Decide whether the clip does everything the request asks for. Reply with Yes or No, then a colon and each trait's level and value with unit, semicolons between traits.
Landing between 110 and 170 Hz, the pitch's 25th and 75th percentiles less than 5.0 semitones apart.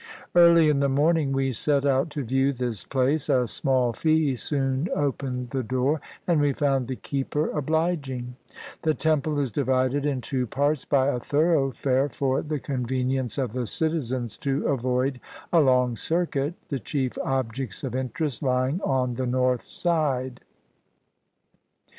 Yes: low, 135 Hz; narrow, 2.6 semitones